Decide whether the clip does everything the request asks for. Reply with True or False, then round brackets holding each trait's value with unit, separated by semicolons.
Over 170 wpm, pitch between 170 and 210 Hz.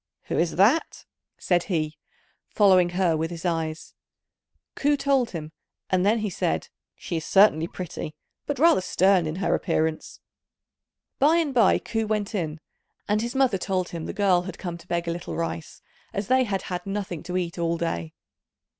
True (180 wpm; 185 Hz)